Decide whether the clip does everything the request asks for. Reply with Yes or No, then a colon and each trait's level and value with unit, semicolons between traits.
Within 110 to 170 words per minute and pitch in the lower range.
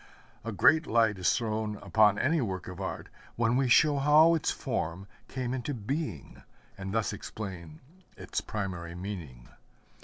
Yes: average, 150 wpm; low, 110 Hz